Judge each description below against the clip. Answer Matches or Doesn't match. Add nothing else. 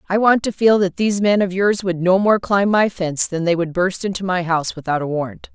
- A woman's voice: Matches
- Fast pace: Matches